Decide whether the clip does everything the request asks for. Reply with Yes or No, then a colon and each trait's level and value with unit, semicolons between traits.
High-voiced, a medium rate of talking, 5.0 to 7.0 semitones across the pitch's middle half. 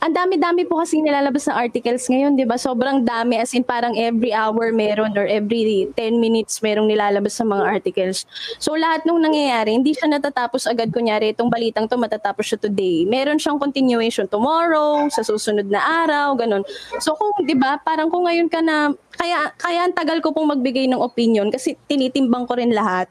No: very high, 250 Hz; fast, 195 wpm; wide, 5.5 semitones